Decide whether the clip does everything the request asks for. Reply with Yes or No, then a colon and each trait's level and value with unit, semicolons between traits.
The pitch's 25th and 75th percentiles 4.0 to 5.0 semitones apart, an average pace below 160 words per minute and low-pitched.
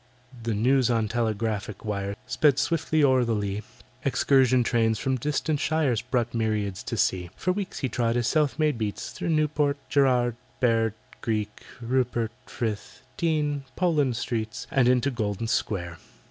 Yes: average, 4.3 semitones; average, 150 wpm; low, 120 Hz